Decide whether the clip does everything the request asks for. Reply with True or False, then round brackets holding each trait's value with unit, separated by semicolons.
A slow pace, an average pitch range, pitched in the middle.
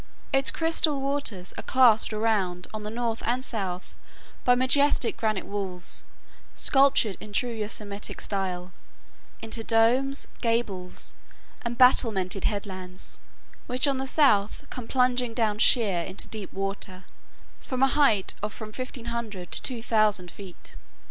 False (130 wpm; 4.2 semitones; 220 Hz)